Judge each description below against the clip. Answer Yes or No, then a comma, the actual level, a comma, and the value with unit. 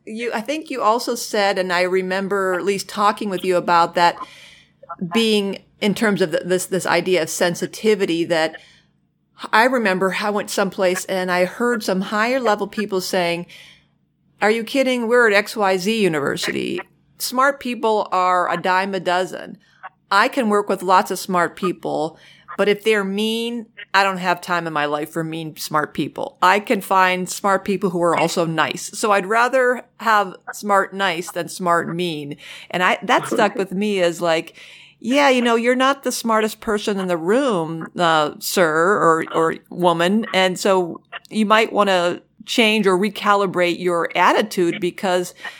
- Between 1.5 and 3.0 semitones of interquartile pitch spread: No, average, 3.5 semitones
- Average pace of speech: Yes, average, 170 wpm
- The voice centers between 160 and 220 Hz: Yes, high, 190 Hz